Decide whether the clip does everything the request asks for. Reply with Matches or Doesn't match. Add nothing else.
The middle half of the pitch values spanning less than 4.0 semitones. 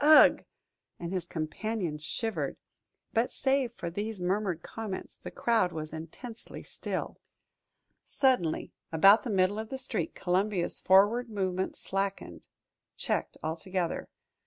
Doesn't match